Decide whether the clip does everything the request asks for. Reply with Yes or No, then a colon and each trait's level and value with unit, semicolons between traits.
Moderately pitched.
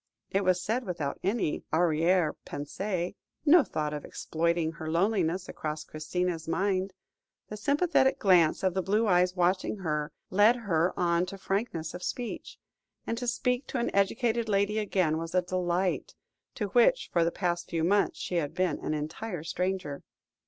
Yes: medium, 180 Hz